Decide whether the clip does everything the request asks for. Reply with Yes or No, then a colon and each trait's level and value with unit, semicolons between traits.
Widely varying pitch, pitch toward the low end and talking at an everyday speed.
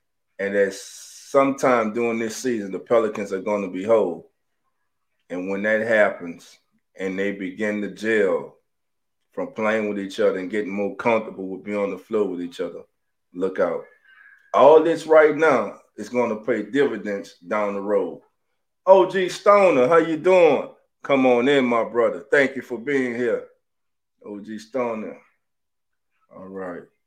Yes: wide, 7.7 semitones; low, 115 Hz; average, 155 wpm